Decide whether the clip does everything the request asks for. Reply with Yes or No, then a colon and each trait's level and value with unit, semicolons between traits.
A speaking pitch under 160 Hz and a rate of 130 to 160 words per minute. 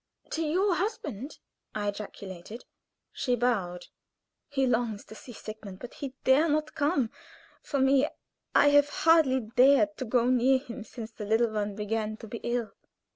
No: high, 245 Hz; average, 155 wpm